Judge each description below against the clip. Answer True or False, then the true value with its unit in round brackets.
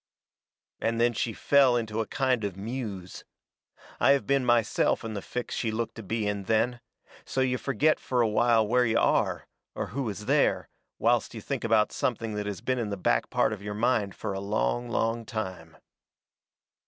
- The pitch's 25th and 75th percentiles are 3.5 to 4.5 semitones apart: False (2.8 semitones)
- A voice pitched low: True (115 Hz)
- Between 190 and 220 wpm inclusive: True (200 wpm)